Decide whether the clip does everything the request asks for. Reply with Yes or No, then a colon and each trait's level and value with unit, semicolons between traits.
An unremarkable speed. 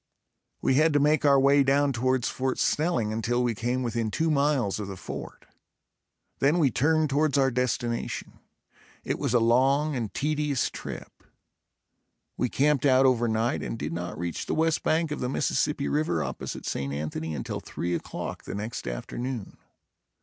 Yes: average, 170 wpm